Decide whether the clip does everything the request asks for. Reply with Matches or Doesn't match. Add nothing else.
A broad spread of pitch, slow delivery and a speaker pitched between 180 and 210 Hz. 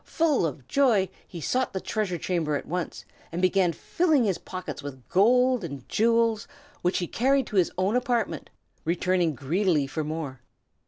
Doesn't match